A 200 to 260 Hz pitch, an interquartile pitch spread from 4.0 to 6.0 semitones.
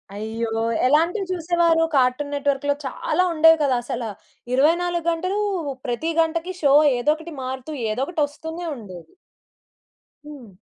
No: very high, 295 Hz; average, 4.6 semitones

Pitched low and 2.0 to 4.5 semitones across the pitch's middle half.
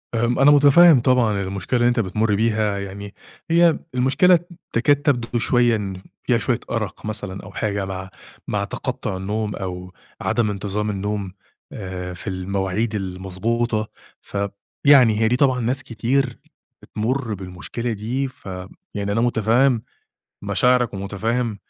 Yes: low, 110 Hz; average, 3.8 semitones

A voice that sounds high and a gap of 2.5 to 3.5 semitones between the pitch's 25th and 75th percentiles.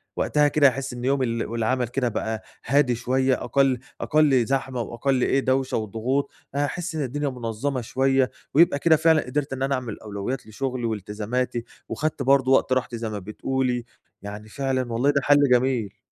No: low, 130 Hz; average, 2.8 semitones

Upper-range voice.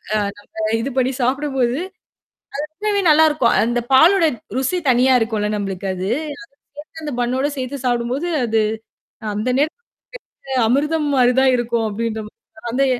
Yes: very high, 255 Hz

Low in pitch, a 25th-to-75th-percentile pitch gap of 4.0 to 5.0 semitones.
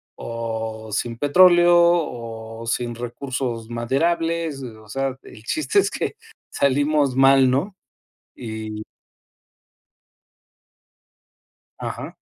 Yes: low, 130 Hz; average, 4.7 semitones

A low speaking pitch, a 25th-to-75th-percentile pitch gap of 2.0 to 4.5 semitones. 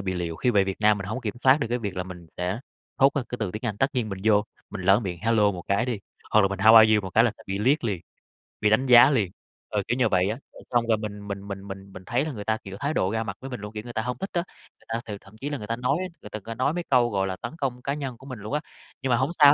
Yes: low, 110 Hz; average, 4.1 semitones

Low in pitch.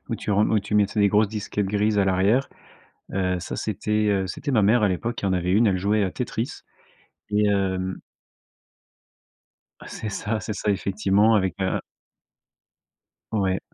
Yes: low, 105 Hz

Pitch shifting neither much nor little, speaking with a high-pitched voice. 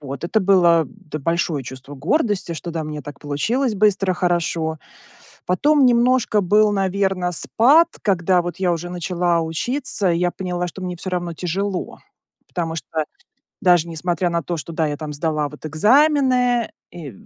No: average, 3.9 semitones; medium, 175 Hz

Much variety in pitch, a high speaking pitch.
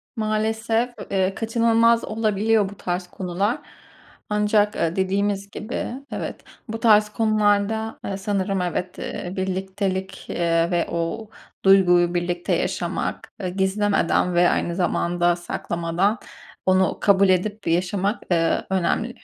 No: average, 3.1 semitones; high, 195 Hz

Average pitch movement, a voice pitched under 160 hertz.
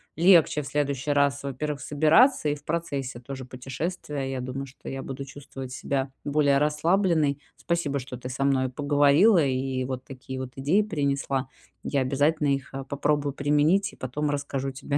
No: narrow, 2.0 semitones; medium, 140 Hz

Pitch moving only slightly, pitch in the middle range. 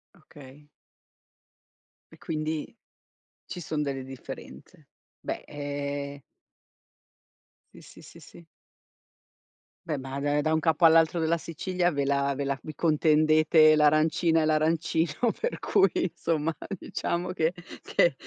Yes: narrow, 2.3 semitones; medium, 155 Hz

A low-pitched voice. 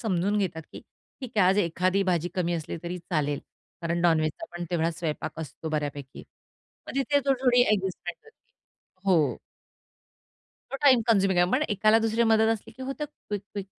No: high, 190 Hz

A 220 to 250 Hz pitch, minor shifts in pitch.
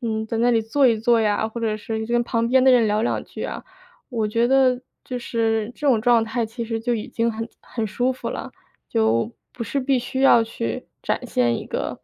Yes: high, 230 Hz; narrow, 1.8 semitones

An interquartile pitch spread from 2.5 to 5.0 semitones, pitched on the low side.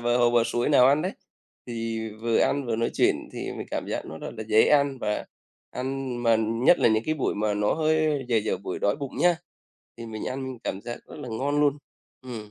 Yes: average, 4.1 semitones; low, 120 Hz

